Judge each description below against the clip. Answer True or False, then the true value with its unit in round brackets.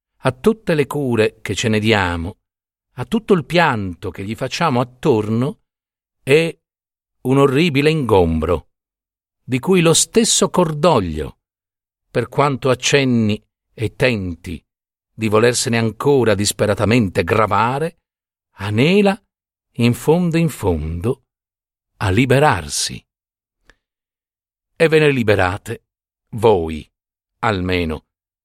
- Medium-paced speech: False (100 wpm)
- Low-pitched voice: True (115 Hz)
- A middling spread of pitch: False (6.9 semitones)